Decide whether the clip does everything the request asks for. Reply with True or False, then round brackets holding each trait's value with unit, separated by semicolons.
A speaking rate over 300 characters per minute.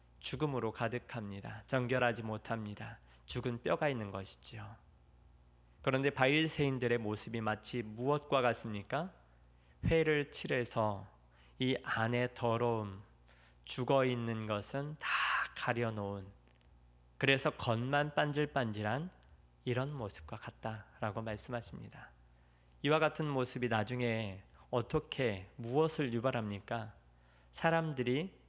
False (255 characters per minute)